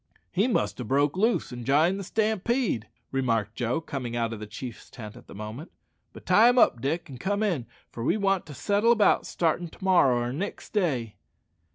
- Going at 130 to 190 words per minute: No, fast, 205 wpm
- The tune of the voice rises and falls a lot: Yes, wide, 8.7 semitones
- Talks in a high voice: No, medium, 145 Hz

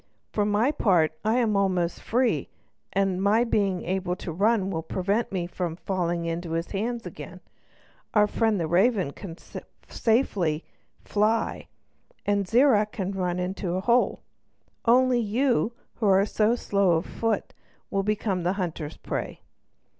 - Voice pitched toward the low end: No, high, 195 Hz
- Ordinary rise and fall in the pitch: Yes, average, 3.7 semitones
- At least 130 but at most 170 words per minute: Yes, average, 155 wpm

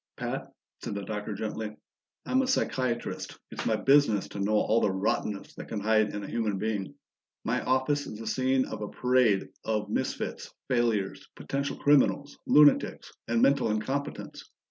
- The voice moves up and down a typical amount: Yes, average, 3.9 semitones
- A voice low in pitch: Yes, low, 110 Hz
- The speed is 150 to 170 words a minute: Yes, average, 165 wpm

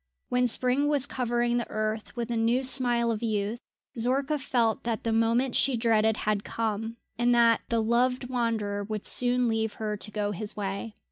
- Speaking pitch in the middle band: No, high, 230 Hz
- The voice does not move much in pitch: Yes, narrow, 2.3 semitones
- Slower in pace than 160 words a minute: No, average, 185 wpm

